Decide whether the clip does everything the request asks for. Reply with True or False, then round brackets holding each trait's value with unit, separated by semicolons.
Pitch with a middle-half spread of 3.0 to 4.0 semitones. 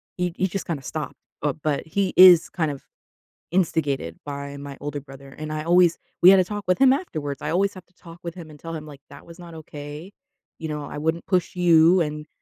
True (3.4 semitones)